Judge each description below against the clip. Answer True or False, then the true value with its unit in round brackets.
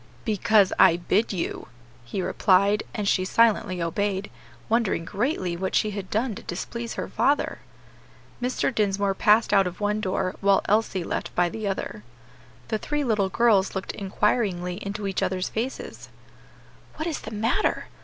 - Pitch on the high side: True (200 Hz)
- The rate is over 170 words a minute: False (155 wpm)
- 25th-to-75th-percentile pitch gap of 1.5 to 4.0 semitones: True (2.8 semitones)